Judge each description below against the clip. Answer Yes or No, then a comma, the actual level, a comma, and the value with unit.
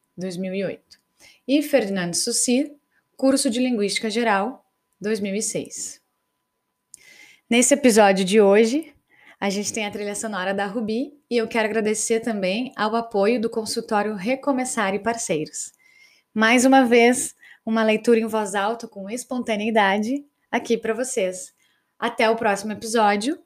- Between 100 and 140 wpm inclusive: Yes, average, 130 wpm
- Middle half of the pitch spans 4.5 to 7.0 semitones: No, average, 3.4 semitones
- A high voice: Yes, high, 225 Hz